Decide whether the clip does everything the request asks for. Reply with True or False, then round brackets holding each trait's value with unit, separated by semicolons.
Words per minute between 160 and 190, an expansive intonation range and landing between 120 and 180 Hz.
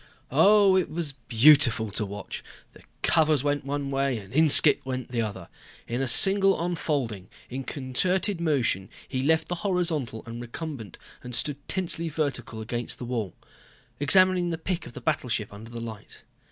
True (165 wpm; 5.9 semitones; 135 Hz)